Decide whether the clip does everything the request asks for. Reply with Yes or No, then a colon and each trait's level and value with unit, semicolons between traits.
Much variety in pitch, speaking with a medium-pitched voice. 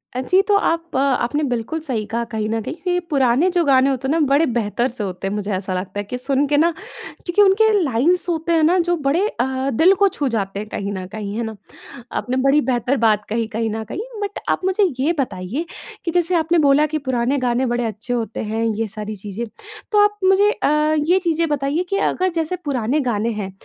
No: wide, 6.9 semitones; very high, 265 Hz